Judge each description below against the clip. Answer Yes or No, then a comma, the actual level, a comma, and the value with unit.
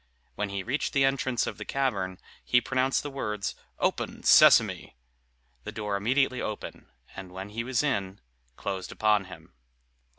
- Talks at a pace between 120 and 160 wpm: Yes, average, 155 wpm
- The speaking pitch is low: Yes, low, 110 Hz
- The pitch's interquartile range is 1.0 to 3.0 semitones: No, average, 5.0 semitones